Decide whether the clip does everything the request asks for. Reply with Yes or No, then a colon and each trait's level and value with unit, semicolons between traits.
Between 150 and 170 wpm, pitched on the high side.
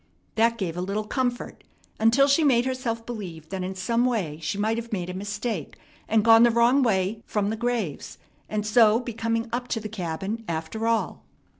No: average, 195 wpm; high, 225 Hz